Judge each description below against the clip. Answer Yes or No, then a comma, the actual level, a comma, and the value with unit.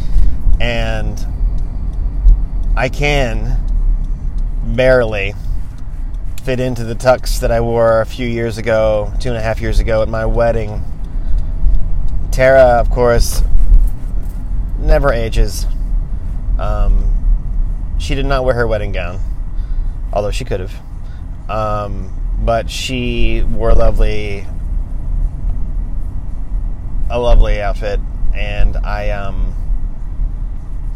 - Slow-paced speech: Yes, slow, 105 wpm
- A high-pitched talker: No, low, 100 Hz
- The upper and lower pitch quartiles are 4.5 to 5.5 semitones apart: Yes, average, 5.2 semitones